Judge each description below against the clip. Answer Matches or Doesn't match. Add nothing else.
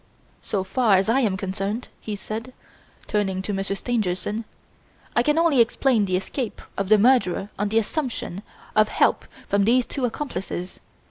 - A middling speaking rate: Matches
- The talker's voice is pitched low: Doesn't match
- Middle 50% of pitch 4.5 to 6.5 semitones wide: Doesn't match